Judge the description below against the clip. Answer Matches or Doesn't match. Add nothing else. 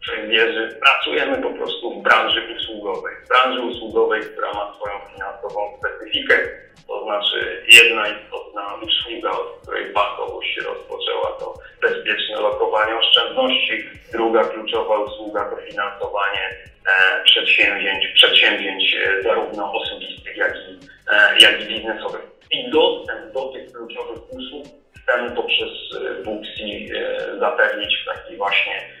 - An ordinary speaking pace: Matches